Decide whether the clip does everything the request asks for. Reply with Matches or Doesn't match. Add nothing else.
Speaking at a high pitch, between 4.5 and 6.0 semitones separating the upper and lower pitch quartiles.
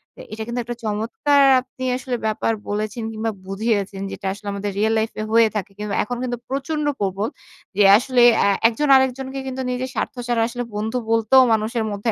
Doesn't match